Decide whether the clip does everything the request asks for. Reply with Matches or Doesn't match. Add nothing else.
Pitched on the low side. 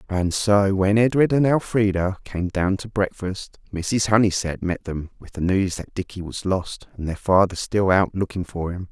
Matches